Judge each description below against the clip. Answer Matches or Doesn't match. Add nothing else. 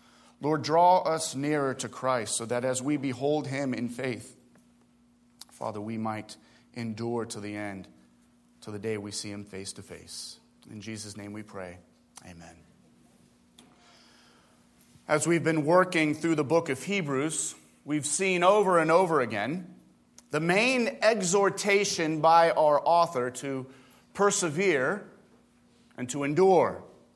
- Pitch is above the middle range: Doesn't match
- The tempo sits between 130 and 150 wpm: Matches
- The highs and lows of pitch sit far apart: Matches